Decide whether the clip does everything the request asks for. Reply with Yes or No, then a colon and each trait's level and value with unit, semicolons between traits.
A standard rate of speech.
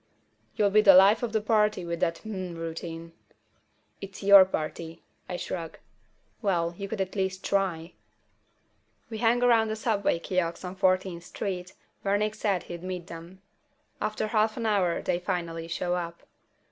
Yes: average, 160 wpm